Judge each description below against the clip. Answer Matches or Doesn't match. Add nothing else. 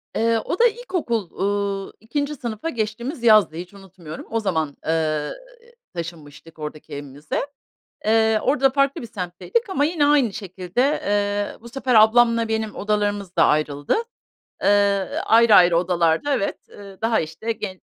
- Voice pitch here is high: Matches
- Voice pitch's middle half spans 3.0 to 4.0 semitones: Doesn't match